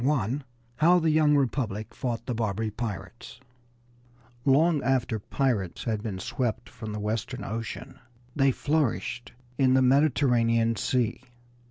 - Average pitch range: Yes, average, 3.6 semitones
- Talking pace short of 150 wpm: Yes, slow, 135 wpm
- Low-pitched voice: Yes, low, 120 Hz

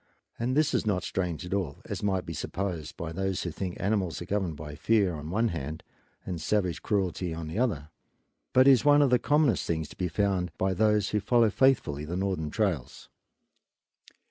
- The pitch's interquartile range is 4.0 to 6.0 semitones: Yes, average, 4.6 semitones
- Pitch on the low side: Yes, very low, 95 Hz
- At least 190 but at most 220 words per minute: Yes, average, 195 wpm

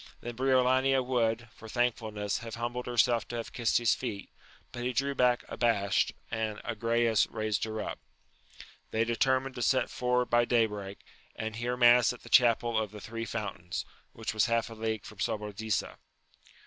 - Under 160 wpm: No, average, 175 wpm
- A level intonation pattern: Yes, narrow, 2.0 semitones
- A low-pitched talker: Yes, low, 115 Hz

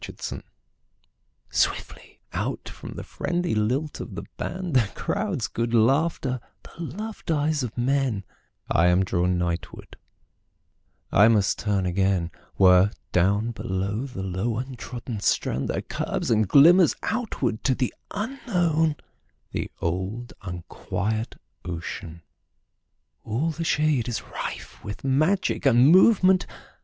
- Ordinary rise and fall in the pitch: No, wide, 8.1 semitones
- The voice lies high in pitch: No, low, 120 Hz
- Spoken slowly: Yes, slow, 110 wpm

